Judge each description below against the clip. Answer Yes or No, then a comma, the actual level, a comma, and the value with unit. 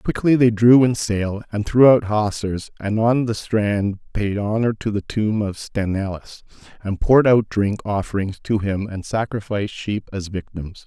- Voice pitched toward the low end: Yes, low, 105 Hz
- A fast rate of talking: No, average, 175 wpm